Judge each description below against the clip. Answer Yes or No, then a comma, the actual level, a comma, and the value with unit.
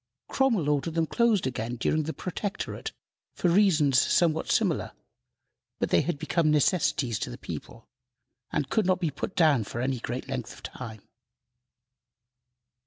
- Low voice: No, medium, 155 Hz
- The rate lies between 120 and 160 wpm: Yes, average, 150 wpm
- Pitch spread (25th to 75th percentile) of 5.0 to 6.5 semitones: Yes, wide, 5.5 semitones